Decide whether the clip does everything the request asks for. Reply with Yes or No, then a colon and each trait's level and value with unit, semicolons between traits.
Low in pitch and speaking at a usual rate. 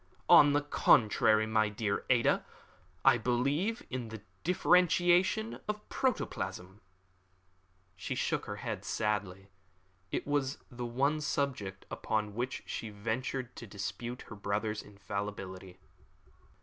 No: low, 115 Hz; slow, 115 wpm